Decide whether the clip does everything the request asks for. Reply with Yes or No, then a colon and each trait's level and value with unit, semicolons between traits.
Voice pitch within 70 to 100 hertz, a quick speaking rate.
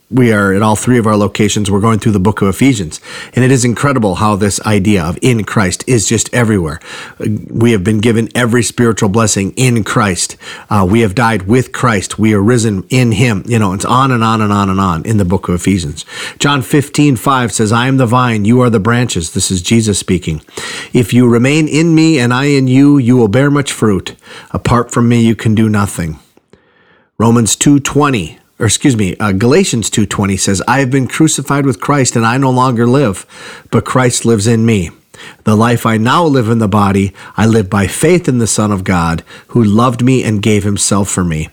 No: low, 115 Hz; fast, 220 wpm